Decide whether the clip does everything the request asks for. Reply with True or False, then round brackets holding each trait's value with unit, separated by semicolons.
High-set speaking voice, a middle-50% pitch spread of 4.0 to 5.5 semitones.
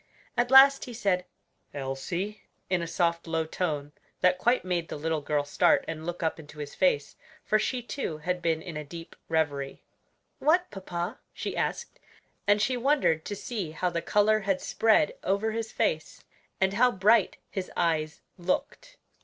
False (180 Hz; 5.2 semitones)